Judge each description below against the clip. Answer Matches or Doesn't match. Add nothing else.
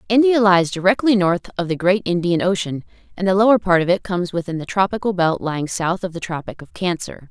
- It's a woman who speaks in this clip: Matches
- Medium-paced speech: Doesn't match